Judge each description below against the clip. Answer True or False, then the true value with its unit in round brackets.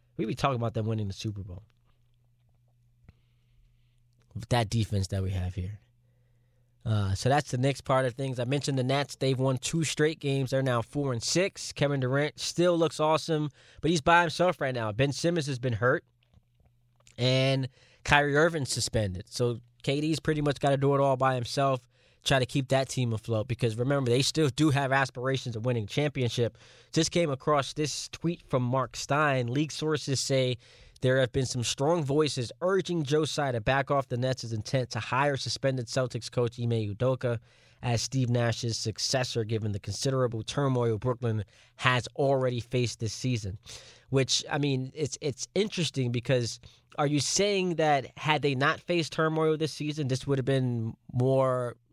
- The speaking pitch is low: True (130 Hz)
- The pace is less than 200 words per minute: True (180 wpm)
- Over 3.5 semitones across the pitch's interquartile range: False (3.1 semitones)